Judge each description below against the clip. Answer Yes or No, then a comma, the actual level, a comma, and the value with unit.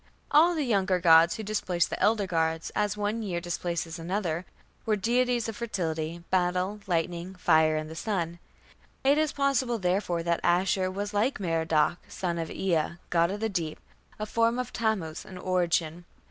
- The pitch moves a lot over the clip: No, average, 4.0 semitones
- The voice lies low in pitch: No, medium, 185 Hz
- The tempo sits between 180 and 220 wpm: No, average, 170 wpm